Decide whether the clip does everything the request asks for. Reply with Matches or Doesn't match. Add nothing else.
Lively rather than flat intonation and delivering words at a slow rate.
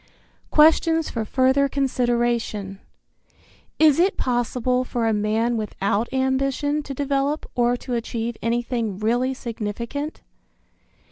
Doesn't match